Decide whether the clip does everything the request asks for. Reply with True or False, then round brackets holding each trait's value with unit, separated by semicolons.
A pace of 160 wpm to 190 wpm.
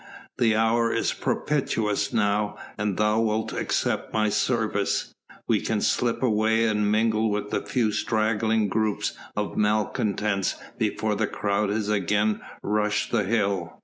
False (140 wpm)